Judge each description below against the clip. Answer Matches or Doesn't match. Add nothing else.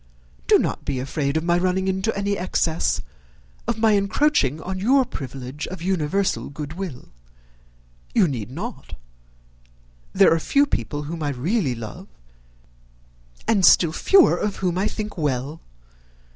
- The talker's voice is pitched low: Doesn't match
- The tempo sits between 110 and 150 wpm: Matches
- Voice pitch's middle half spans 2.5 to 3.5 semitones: Doesn't match